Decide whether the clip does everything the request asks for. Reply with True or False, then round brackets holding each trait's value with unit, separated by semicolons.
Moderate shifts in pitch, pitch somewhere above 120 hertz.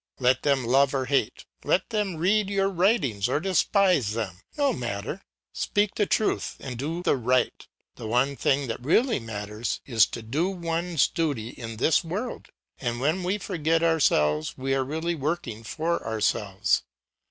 False (7.0 semitones; 140 Hz)